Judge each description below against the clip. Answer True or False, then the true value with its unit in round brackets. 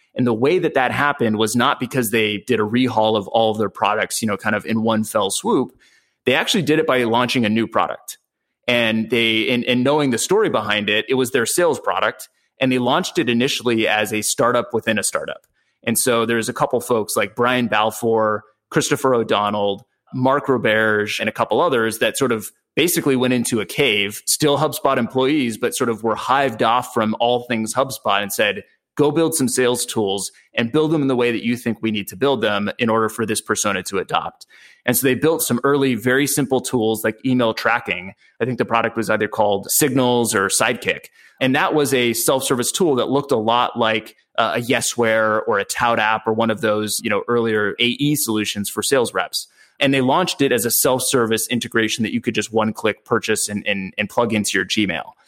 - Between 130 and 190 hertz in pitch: False (120 Hz)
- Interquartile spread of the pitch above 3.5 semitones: False (2.9 semitones)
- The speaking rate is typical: False (215 wpm)